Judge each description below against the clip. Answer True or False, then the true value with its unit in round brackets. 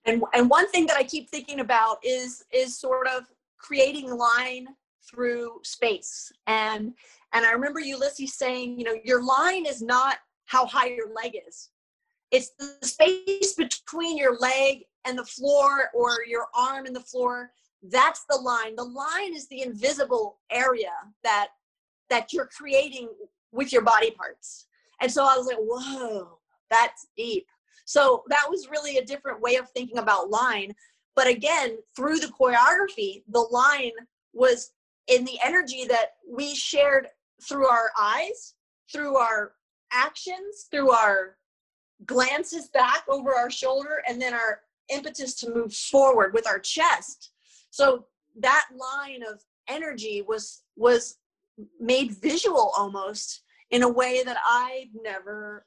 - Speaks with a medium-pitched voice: False (260 Hz)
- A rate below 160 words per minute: True (150 wpm)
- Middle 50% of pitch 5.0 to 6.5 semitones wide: False (4.6 semitones)